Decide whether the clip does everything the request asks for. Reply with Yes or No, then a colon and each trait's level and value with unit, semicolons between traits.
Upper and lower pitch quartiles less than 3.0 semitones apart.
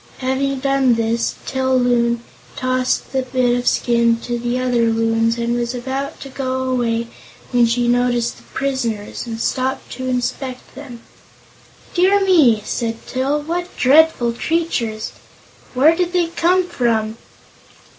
Yes: narrow, 2.6 semitones